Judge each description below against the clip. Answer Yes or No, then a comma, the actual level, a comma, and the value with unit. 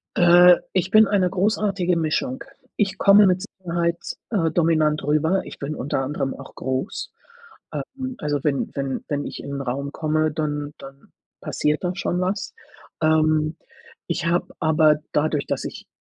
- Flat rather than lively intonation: No, average, 3.7 semitones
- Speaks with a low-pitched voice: No, medium, 160 Hz